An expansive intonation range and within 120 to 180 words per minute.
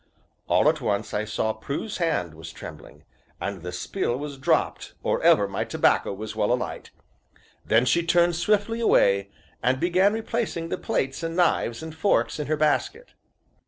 Yes: wide, 8.3 semitones; average, 165 wpm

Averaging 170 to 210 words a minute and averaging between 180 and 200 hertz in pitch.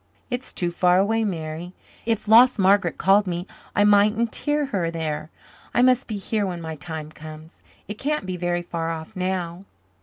Yes: average, 180 wpm; medium, 185 Hz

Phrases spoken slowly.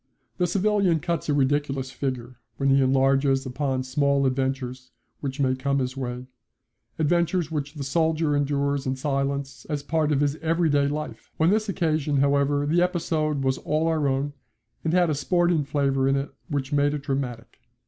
No: average, 170 wpm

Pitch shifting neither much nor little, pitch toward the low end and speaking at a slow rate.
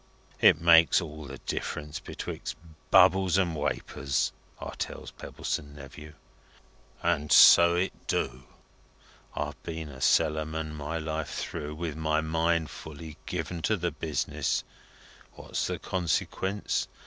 No: narrow, 2.1 semitones; very low, 80 Hz; slow, 125 wpm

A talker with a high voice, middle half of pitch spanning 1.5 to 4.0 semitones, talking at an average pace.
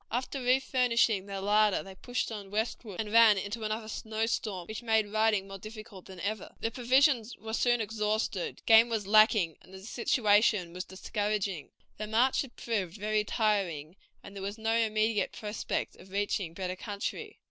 Yes: high, 215 Hz; narrow, 2.4 semitones; average, 170 wpm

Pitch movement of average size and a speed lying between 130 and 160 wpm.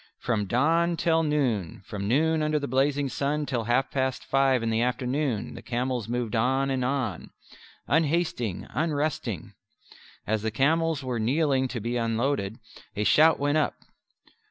Yes: average, 4.2 semitones; average, 155 wpm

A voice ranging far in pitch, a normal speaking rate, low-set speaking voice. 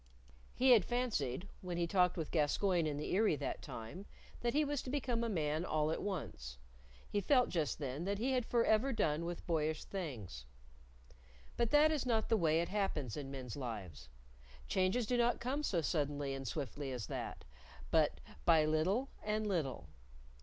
No: wide, 7.7 semitones; average, 180 wpm; medium, 175 Hz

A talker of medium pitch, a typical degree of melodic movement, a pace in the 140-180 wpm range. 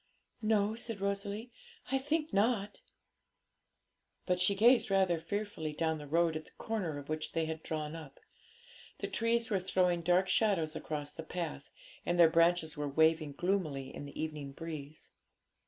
Yes: medium, 170 Hz; average, 4.5 semitones; average, 160 wpm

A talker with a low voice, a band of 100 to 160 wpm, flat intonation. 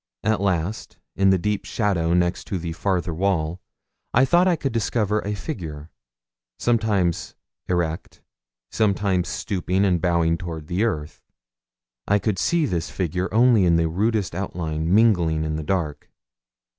No: very low, 95 Hz; average, 145 wpm; average, 4.0 semitones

